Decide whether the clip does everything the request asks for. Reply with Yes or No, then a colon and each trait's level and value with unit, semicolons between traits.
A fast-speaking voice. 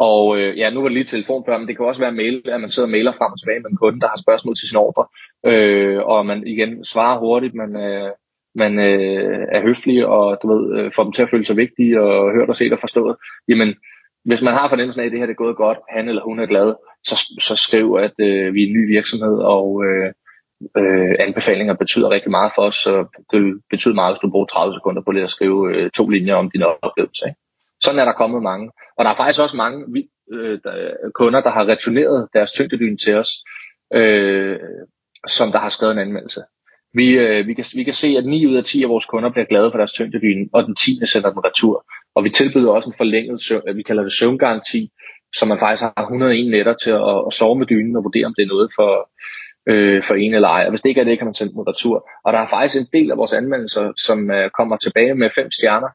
Yes: fast, 250 wpm